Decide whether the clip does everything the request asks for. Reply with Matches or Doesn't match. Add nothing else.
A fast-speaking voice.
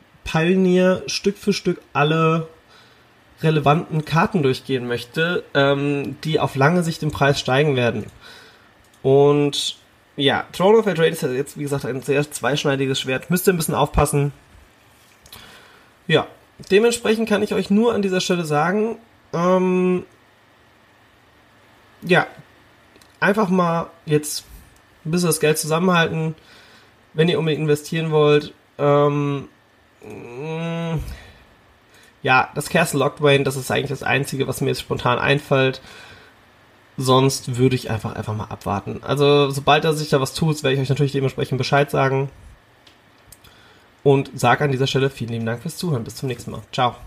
Doesn't match